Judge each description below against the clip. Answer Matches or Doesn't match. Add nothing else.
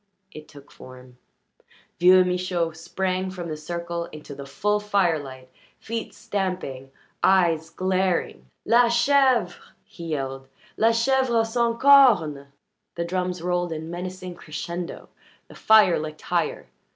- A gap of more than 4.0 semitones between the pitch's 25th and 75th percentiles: Matches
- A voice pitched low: Doesn't match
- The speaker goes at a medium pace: Doesn't match